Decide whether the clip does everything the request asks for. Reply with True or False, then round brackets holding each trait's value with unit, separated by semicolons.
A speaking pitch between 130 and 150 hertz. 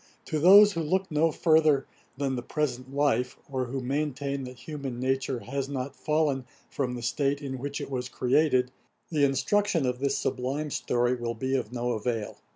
True (135 Hz)